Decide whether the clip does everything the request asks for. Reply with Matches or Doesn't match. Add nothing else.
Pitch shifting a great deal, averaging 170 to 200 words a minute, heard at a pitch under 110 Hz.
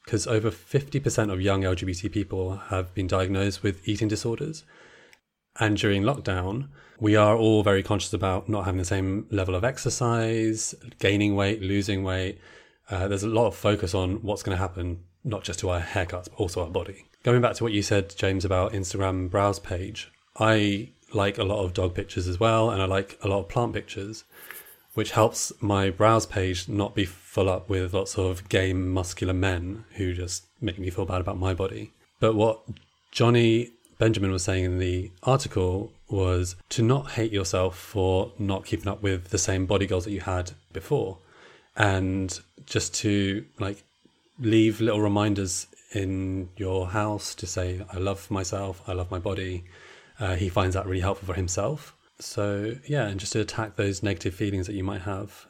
Doesn't match